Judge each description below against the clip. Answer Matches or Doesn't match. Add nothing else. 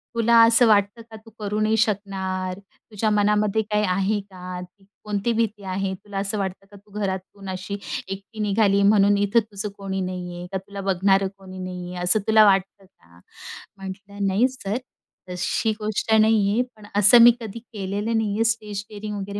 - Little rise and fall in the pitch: Matches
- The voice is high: Matches